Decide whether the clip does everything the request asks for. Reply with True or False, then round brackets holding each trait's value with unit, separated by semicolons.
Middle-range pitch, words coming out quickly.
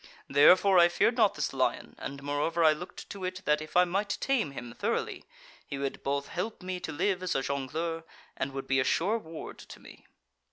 True (165 Hz; 210 wpm)